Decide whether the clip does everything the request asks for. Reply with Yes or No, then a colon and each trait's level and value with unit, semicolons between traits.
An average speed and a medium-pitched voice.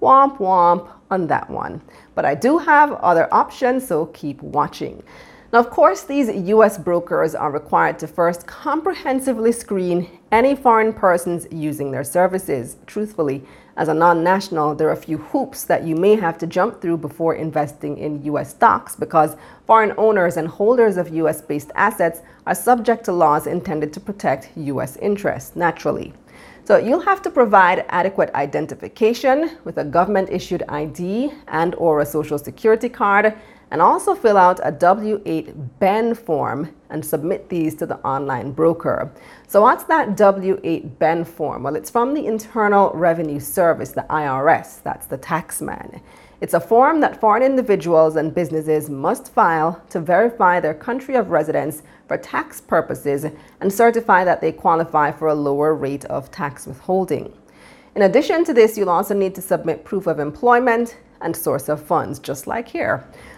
Yes: average, 170 wpm; medium, 180 Hz